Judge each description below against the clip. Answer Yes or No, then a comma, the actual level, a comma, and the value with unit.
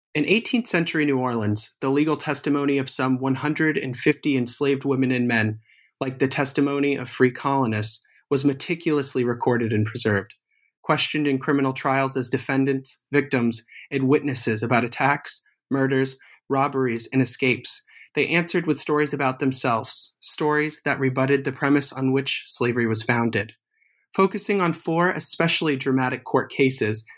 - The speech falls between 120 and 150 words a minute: Yes, average, 140 wpm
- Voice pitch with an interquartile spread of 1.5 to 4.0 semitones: Yes, narrow, 2.6 semitones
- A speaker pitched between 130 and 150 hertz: Yes, low, 135 Hz